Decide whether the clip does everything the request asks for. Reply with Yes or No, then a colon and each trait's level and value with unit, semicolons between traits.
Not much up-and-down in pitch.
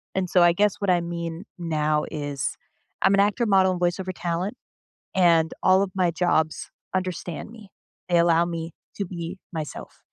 Yes: narrow, 2.3 semitones